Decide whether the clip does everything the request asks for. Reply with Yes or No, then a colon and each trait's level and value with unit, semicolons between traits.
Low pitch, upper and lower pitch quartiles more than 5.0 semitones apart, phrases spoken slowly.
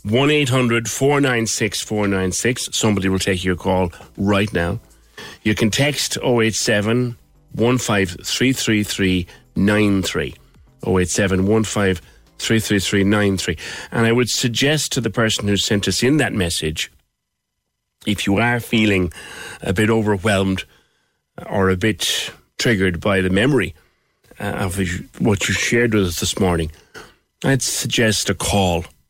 No: low, 105 Hz; average, 3.8 semitones; slow, 115 wpm